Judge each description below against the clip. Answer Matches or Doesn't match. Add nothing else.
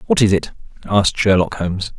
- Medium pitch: Doesn't match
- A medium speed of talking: Matches